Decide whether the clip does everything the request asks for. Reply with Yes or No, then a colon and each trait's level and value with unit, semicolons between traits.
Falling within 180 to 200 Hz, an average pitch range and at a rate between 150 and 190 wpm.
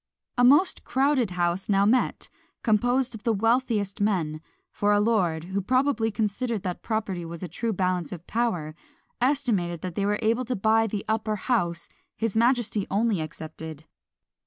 No: high, 210 Hz; average, 4.6 semitones; average, 160 wpm